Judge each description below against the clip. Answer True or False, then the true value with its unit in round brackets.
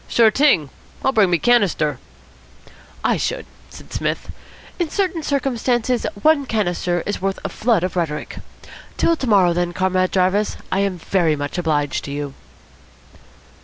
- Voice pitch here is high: True (195 Hz)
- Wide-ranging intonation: True (5.8 semitones)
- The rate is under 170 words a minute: True (150 wpm)